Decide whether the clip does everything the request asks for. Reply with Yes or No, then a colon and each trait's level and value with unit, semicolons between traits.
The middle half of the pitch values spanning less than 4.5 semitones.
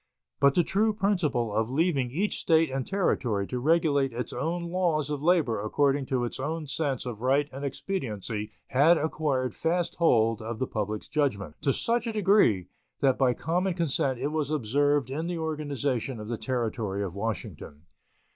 No: wide, 5.6 semitones